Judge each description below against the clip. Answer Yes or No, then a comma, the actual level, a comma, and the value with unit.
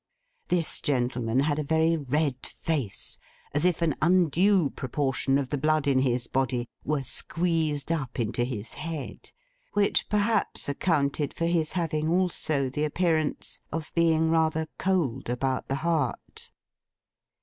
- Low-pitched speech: No, medium, 150 Hz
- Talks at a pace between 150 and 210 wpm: No, average, 140 wpm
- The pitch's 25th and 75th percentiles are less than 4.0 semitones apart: Yes, average, 3.6 semitones